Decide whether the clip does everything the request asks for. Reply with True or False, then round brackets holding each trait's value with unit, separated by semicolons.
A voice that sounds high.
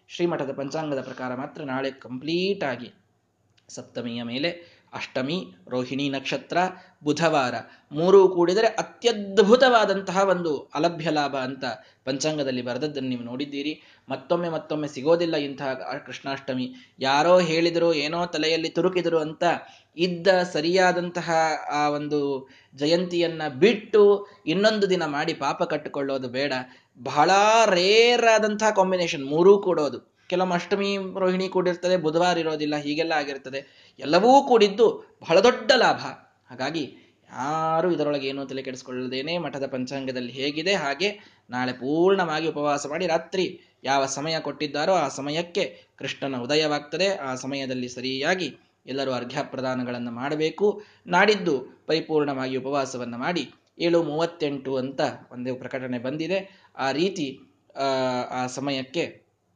False (155 Hz)